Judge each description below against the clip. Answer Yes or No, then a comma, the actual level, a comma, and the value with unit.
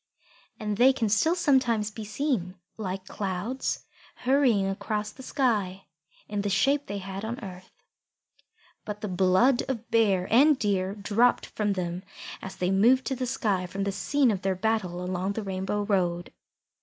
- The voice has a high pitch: Yes, high, 205 Hz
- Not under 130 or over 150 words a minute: No, average, 170 wpm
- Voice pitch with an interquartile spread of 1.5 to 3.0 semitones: No, average, 4.0 semitones